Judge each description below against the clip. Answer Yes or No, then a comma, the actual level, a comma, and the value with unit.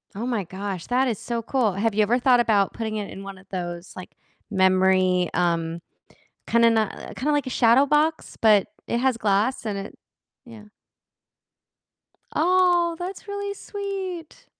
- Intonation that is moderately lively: No, wide, 5.8 semitones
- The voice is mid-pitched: No, high, 225 Hz